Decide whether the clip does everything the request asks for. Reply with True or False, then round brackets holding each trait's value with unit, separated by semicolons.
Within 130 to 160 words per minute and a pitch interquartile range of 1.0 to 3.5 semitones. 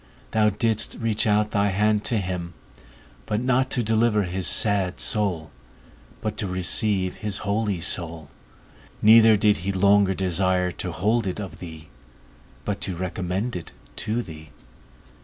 True (150 wpm; 2.9 semitones)